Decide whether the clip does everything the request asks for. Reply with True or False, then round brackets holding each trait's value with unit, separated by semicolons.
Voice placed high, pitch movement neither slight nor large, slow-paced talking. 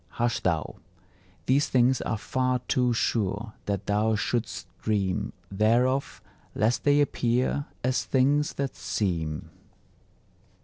False (115 Hz; 4.0 semitones; 115 wpm)